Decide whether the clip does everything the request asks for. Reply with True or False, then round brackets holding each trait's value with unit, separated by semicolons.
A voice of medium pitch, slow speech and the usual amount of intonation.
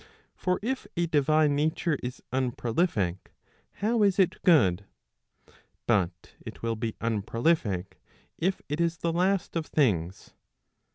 False (145 Hz; 125 wpm; 7.4 semitones)